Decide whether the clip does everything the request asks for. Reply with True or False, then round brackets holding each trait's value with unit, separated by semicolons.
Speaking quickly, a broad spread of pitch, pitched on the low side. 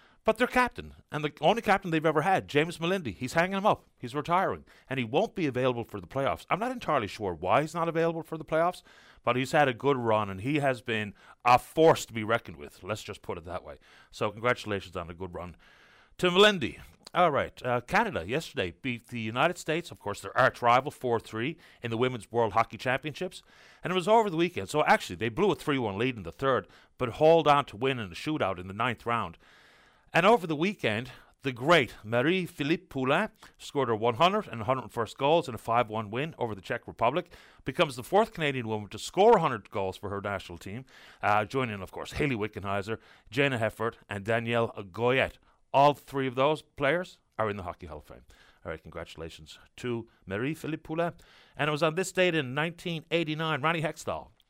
True (210 wpm; 6.6 semitones; 130 Hz)